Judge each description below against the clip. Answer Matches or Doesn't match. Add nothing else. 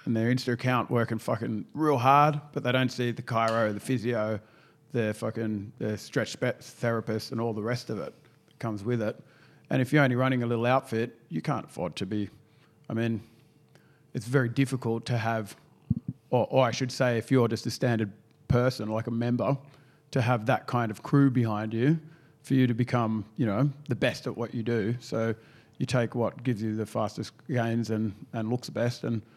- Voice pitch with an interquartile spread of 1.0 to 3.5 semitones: Matches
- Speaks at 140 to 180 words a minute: Doesn't match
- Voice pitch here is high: Doesn't match